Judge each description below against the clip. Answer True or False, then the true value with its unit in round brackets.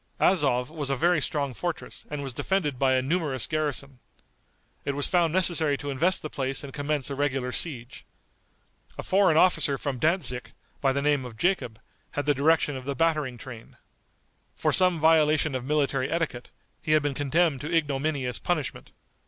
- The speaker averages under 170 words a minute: False (175 wpm)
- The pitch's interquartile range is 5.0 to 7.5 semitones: False (3.1 semitones)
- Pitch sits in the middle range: True (145 Hz)